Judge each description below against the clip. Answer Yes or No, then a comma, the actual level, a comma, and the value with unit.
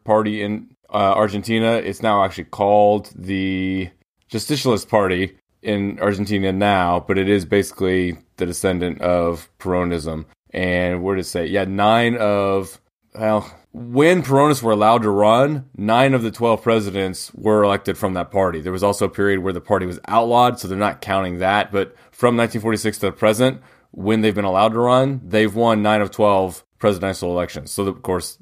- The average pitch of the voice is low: Yes, low, 100 Hz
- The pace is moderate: Yes, average, 180 wpm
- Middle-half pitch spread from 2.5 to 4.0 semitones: Yes, average, 2.8 semitones